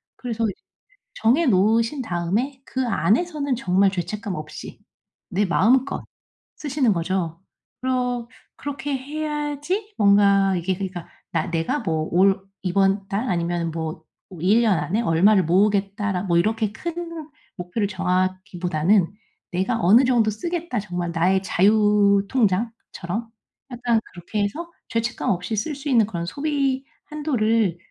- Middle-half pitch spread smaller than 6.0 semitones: Yes, wide, 5.6 semitones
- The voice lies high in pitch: Yes, high, 210 Hz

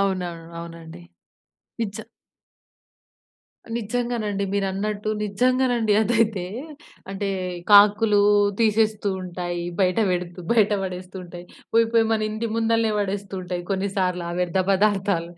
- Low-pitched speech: No, high, 200 Hz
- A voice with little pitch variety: No, average, 3.1 semitones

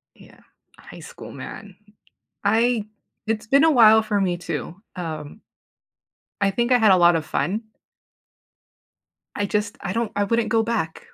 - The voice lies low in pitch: No, high, 210 Hz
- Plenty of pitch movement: No, average, 3.6 semitones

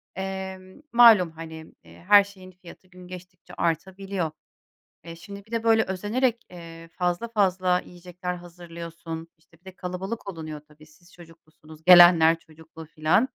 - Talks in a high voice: No, medium, 180 Hz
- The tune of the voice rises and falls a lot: No, narrow, 2.6 semitones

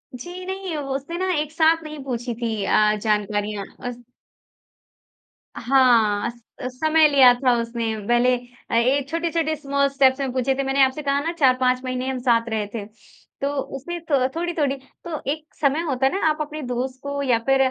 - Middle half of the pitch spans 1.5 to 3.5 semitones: No, average, 3.9 semitones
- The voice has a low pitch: No, very high, 270 Hz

